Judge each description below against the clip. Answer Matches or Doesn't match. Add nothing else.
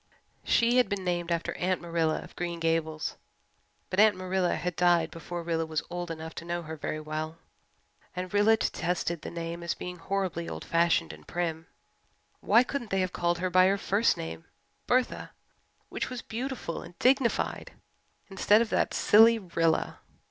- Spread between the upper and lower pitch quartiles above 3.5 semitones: Doesn't match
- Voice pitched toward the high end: Doesn't match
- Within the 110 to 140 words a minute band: Doesn't match